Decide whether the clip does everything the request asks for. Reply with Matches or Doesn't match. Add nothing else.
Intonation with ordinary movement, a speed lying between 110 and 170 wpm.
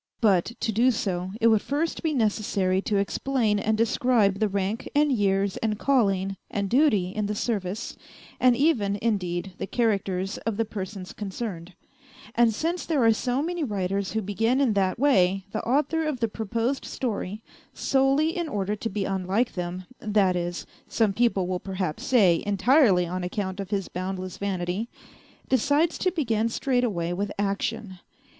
Matches